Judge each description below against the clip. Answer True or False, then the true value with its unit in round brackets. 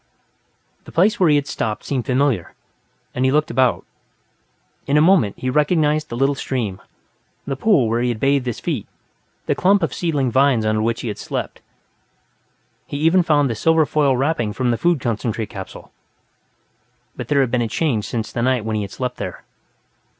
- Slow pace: False (185 wpm)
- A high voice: False (130 Hz)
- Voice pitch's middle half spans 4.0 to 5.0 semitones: True (4.6 semitones)